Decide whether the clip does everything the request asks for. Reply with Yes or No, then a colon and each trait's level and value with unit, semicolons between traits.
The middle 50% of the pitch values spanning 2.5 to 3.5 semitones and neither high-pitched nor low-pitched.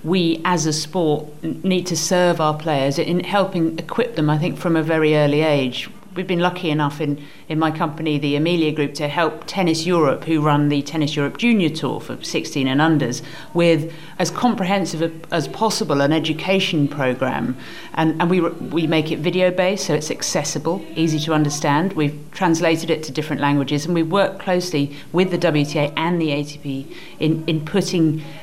Yes: average, 2.8 semitones; medium, 160 Hz